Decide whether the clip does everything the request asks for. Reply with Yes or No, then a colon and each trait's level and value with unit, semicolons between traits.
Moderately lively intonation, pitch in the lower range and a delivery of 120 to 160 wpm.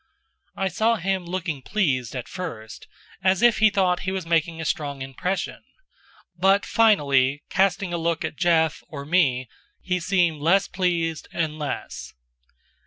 No: average, 4.1 semitones; medium, 170 Hz; average, 150 wpm